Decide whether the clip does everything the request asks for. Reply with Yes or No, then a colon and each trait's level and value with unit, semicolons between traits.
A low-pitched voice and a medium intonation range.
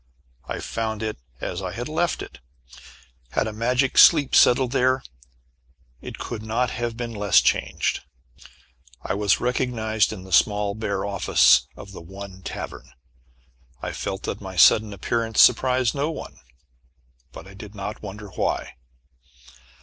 Yes: low, 110 Hz; average, 3.6 semitones